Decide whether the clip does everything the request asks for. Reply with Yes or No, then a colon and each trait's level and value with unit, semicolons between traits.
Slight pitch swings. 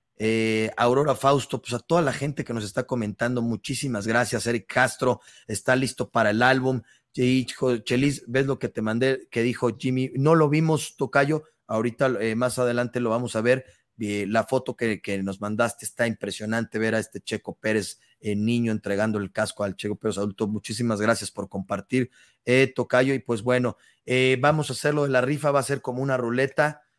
No: average, 3.1 semitones